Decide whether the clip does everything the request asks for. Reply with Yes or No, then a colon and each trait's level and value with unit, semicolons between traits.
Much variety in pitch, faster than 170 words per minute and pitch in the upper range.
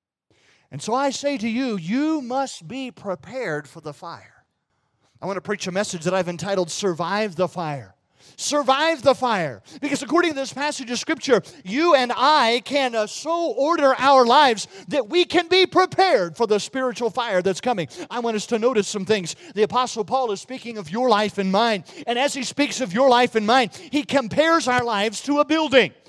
Yes: wide, 5.7 semitones; average, 200 wpm; high, 245 Hz